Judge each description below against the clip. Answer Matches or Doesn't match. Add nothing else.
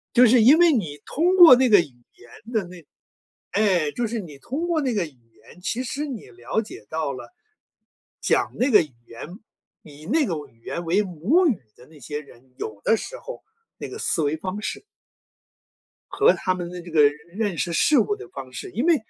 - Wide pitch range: Matches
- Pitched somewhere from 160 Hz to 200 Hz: Matches